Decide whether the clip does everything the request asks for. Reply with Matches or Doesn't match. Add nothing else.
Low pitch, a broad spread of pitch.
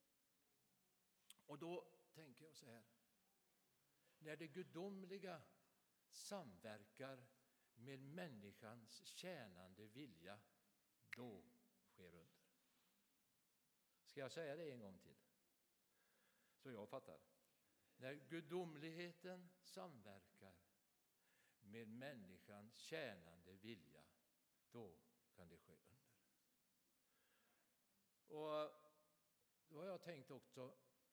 Doesn't match